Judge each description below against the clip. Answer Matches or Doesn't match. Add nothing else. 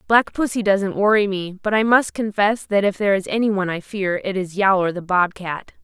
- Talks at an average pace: Doesn't match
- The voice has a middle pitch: Doesn't match